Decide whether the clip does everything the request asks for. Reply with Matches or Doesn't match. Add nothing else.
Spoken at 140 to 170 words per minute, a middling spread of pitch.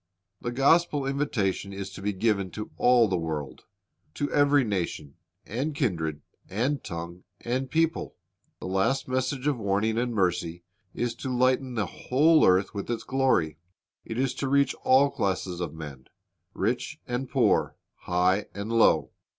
Doesn't match